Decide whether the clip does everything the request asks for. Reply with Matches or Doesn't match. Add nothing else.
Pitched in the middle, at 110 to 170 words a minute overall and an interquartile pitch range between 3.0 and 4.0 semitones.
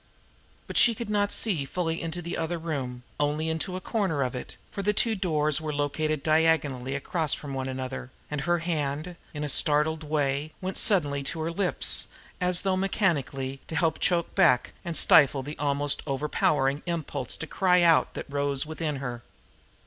Doesn't match